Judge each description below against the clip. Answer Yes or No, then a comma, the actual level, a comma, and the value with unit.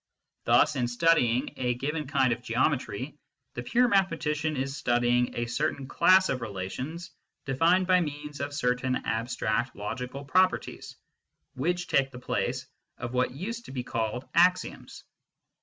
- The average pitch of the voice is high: No, low, 135 Hz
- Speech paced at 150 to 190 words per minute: No, average, 140 wpm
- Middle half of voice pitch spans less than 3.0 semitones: No, average, 4.9 semitones